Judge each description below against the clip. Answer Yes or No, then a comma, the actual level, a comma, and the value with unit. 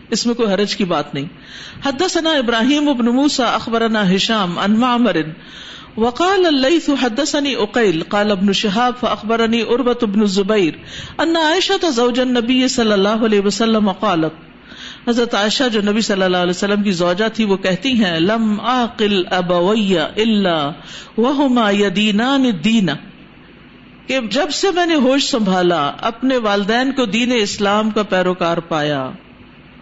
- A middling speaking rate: No, slow, 100 wpm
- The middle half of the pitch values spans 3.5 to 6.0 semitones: Yes, average, 3.9 semitones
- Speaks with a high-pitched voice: Yes, high, 225 Hz